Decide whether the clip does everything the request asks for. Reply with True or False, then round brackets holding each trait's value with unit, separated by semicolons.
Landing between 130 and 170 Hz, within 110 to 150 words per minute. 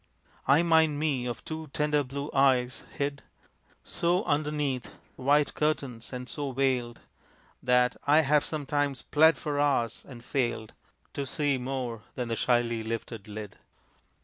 True (135 Hz; 140 wpm)